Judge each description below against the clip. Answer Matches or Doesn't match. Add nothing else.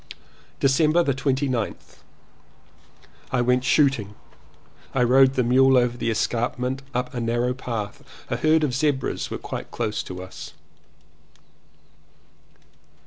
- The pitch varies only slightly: Matches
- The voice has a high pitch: Doesn't match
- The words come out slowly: Matches